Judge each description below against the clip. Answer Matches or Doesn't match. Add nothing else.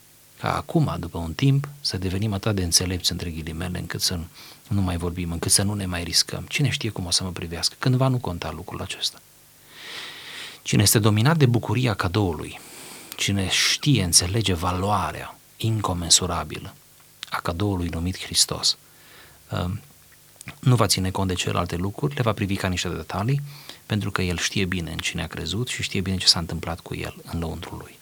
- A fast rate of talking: Matches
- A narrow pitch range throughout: Doesn't match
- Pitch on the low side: Matches